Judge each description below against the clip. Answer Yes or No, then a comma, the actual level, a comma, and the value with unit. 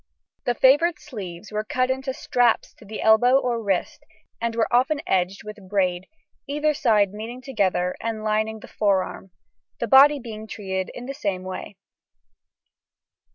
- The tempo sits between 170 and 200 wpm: No, average, 155 wpm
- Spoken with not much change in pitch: No, average, 4.3 semitones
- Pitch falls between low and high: No, high, 220 Hz